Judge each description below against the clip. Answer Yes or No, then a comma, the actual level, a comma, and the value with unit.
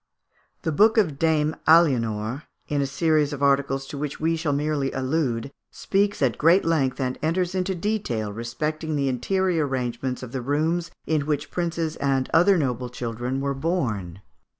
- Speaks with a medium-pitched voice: Yes, medium, 145 Hz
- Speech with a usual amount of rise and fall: Yes, average, 4.1 semitones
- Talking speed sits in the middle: Yes, average, 165 wpm